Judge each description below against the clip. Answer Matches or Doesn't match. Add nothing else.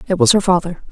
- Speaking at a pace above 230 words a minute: Matches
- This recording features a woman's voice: Matches